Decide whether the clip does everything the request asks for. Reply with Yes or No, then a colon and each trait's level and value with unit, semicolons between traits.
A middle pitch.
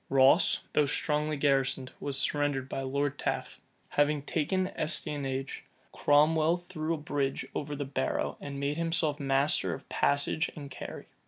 Yes: medium, 145 Hz